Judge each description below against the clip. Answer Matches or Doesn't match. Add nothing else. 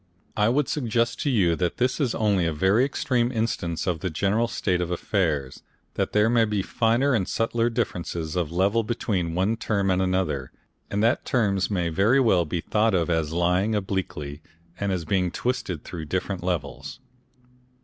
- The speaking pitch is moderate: Doesn't match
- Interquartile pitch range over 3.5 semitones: Matches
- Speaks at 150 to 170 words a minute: Doesn't match